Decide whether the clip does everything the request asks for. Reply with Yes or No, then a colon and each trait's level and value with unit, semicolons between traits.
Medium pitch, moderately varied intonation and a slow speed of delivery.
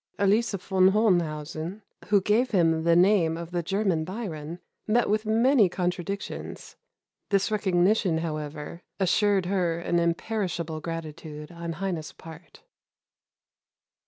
Yes: medium, 180 Hz; average, 3.6 semitones; slow, 115 wpm